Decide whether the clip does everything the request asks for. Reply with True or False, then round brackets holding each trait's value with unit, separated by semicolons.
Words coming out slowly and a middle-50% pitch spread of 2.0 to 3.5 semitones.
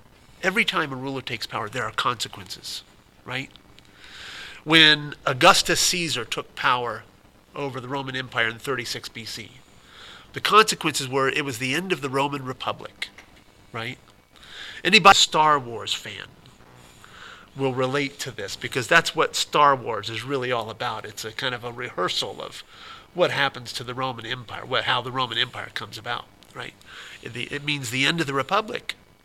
False (165 wpm; 3.2 semitones)